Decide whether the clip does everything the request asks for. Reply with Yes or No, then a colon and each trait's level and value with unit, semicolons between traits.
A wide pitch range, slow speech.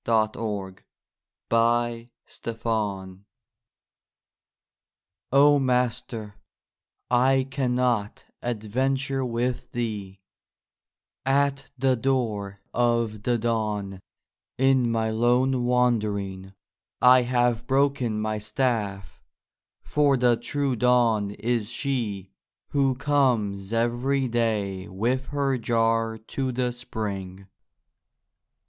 No: average, 3.2 semitones; slow, 90 wpm